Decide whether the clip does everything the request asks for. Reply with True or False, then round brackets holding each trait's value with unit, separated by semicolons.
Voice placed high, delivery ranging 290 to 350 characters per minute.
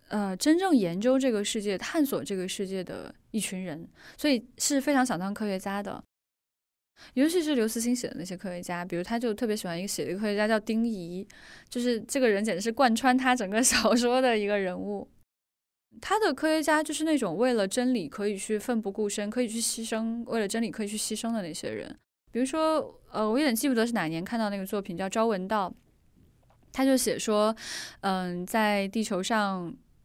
True (220 Hz; 305 characters per minute)